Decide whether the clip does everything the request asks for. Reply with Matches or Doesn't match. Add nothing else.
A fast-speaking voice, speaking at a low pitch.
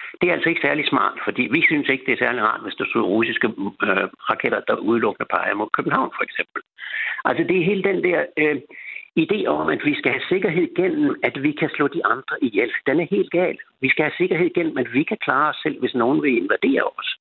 Doesn't match